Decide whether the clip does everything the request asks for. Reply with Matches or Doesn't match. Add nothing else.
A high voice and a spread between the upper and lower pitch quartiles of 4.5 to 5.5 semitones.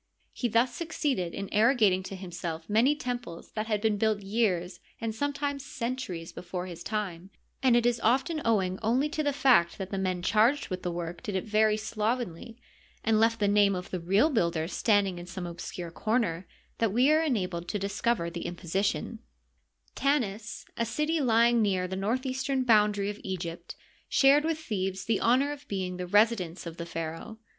Matches